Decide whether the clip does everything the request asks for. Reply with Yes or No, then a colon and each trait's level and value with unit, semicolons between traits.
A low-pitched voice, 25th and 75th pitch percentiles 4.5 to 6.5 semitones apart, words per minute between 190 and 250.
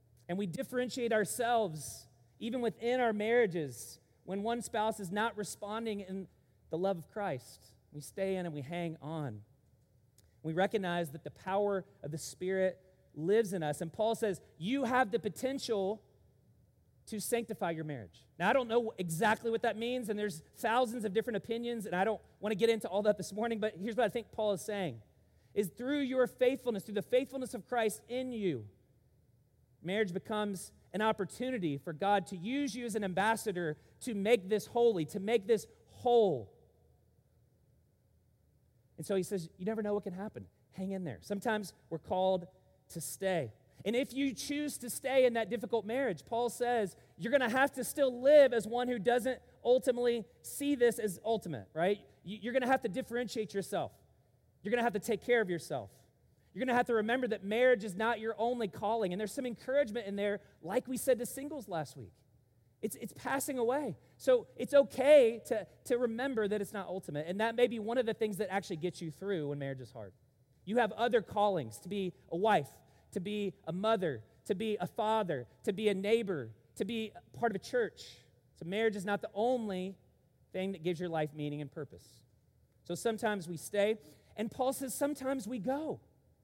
No: high, 210 Hz; wide, 5.6 semitones; average, 195 wpm